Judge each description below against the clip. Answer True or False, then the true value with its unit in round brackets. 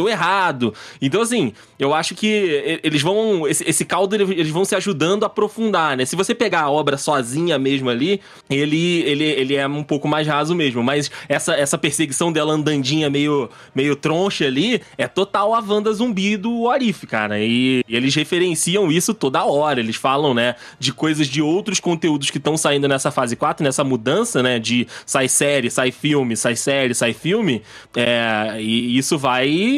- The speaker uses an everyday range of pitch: False (5.9 semitones)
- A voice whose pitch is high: False (150 Hz)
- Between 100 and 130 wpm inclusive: False (185 wpm)